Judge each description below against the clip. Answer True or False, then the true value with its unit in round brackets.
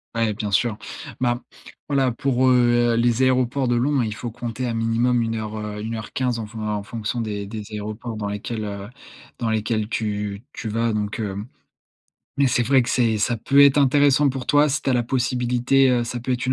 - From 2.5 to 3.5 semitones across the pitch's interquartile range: True (2.8 semitones)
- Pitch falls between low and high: False (120 Hz)